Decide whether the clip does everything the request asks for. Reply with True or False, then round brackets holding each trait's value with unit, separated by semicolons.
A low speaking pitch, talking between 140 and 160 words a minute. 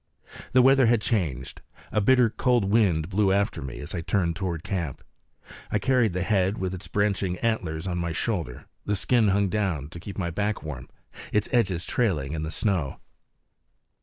False (95 Hz; 180 wpm)